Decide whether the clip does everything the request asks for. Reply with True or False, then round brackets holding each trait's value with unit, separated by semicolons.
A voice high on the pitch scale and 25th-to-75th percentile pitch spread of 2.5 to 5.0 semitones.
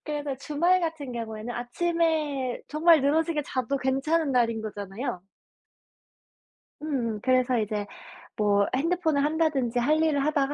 True (275 Hz; 4.5 semitones)